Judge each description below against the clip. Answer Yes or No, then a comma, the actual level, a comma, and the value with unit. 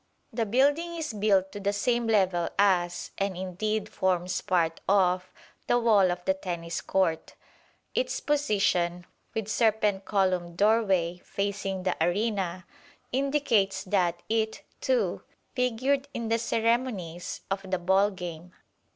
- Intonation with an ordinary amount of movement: Yes, average, 3.8 semitones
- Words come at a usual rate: No, slow, 130 wpm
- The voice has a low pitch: No, high, 195 Hz